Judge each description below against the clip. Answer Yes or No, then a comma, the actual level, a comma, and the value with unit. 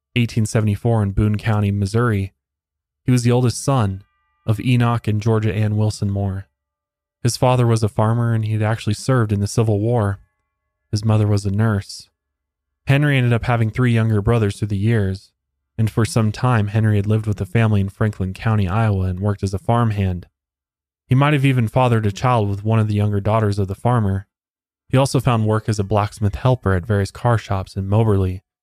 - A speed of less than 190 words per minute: No, average, 200 wpm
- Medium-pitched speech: No, low, 105 Hz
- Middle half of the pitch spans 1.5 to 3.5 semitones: Yes, average, 2.9 semitones